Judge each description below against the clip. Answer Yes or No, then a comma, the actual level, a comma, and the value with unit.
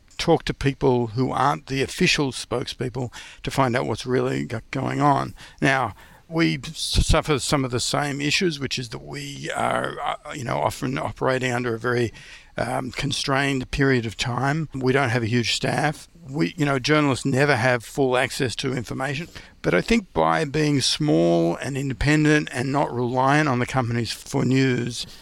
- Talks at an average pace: Yes, average, 170 wpm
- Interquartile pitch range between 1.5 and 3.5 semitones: Yes, average, 3.0 semitones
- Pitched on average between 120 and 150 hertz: Yes, low, 135 Hz